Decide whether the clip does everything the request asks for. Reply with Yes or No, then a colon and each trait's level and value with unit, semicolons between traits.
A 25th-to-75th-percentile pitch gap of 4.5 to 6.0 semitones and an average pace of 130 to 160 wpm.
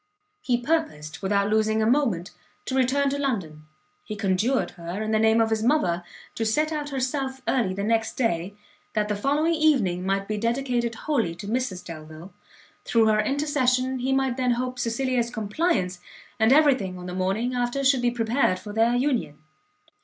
No: average, 4.8 semitones; average, 180 wpm